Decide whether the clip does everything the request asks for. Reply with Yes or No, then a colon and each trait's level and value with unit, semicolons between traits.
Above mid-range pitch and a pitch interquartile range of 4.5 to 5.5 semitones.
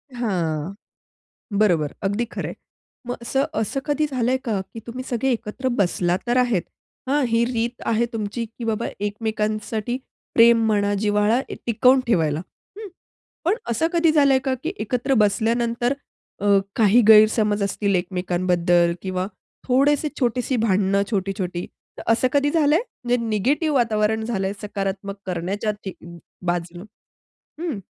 No: high, 220 Hz; average, 3.9 semitones